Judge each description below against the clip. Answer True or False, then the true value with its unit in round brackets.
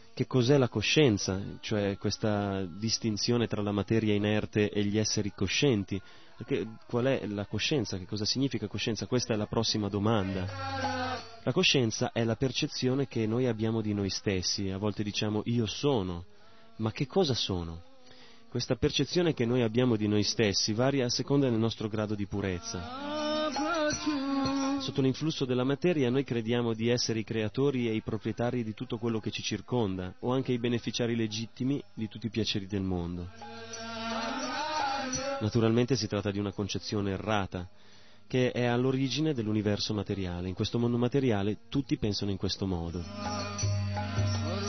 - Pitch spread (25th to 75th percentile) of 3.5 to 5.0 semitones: True (3.9 semitones)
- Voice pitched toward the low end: True (115 Hz)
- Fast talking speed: False (155 wpm)